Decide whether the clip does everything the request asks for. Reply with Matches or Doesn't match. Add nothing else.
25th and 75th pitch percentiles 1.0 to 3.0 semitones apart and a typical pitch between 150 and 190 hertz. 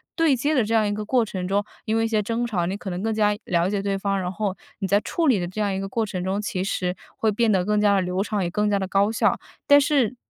Doesn't match